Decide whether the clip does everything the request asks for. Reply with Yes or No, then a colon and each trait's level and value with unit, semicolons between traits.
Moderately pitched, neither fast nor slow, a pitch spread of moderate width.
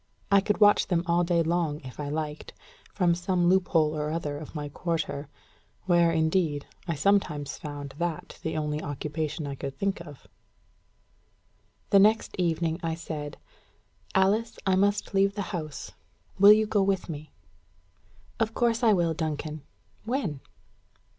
Yes: medium, 170 Hz; average, 150 wpm; average, 4.3 semitones